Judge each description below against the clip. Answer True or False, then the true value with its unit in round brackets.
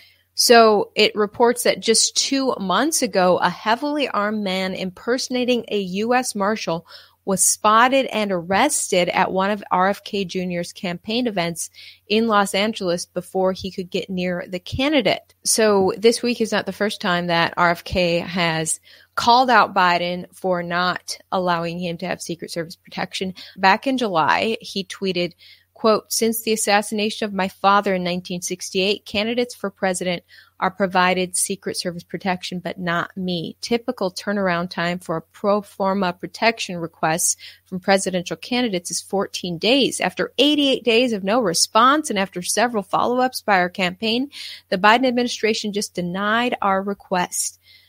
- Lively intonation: False (3.7 semitones)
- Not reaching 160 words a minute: True (150 wpm)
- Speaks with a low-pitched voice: False (195 Hz)